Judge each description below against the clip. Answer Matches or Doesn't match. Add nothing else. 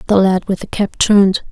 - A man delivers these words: Doesn't match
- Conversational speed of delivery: Doesn't match